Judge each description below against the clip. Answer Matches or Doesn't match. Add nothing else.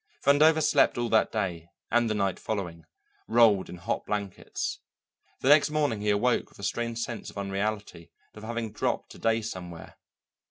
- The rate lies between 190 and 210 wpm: Doesn't match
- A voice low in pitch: Matches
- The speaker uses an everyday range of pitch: Matches